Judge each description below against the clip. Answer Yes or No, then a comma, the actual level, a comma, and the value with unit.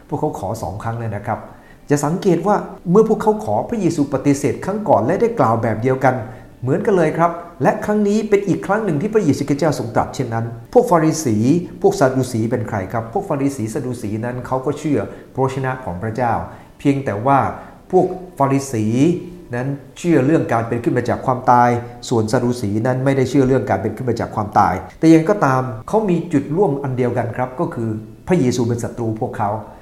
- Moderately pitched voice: No, low, 130 Hz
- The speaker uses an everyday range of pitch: No, wide, 5.8 semitones